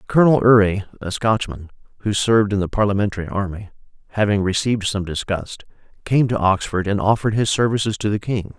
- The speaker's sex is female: No, male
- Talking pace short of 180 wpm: Yes, average, 170 wpm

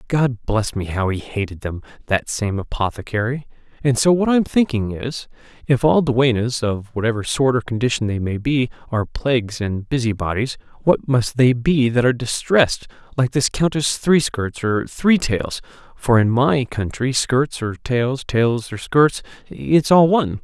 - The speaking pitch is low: Yes, low, 125 Hz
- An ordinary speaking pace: Yes, average, 170 wpm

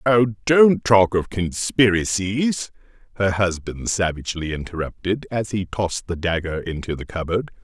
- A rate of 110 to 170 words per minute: Yes, slow, 135 wpm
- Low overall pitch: Yes, low, 100 Hz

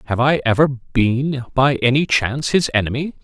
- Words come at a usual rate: Yes, average, 165 wpm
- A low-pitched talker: Yes, low, 130 Hz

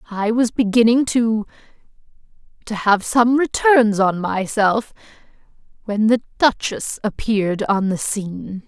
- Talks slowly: Yes, slow, 110 wpm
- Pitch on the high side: Yes, high, 220 Hz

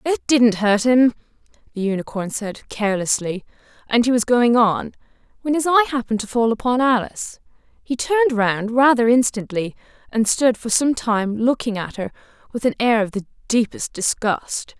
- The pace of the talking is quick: No, average, 165 wpm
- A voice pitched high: Yes, high, 230 Hz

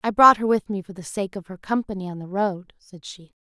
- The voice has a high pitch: Yes, high, 195 Hz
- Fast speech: Yes, fast, 280 wpm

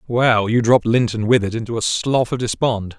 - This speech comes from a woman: No, male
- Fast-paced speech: Yes, fast, 220 wpm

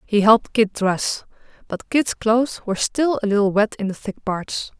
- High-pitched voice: Yes, high, 215 Hz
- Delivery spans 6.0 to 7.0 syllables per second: No, 4.9 syllables/s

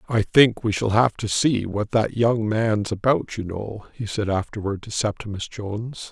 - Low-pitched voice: Yes, low, 110 Hz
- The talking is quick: No, average, 195 wpm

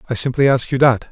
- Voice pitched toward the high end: No, low, 130 Hz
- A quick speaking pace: Yes, fast, 270 wpm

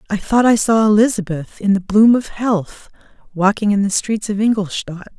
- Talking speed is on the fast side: No, average, 185 wpm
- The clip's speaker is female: Yes, female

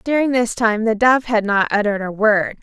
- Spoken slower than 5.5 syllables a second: Yes, 5.3 syllables/s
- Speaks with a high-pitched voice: Yes, high, 225 Hz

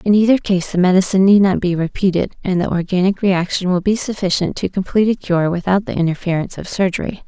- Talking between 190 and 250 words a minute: Yes, fast, 205 wpm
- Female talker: Yes, female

